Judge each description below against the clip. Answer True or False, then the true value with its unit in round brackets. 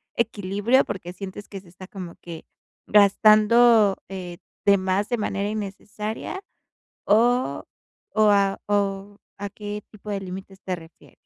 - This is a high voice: True (200 Hz)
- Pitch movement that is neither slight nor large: False (1.8 semitones)